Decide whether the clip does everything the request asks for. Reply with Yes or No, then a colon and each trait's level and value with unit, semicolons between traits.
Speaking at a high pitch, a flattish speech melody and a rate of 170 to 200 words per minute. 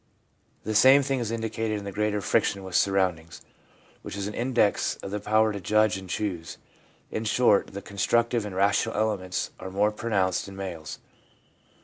No: low, 105 Hz; narrow, 2.3 semitones; average, 175 wpm